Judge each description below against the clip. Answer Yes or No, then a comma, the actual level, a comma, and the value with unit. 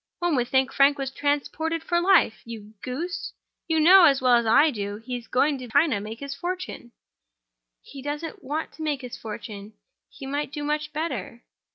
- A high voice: Yes, very high, 280 Hz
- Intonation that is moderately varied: Yes, average, 4.7 semitones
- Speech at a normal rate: Yes, average, 190 wpm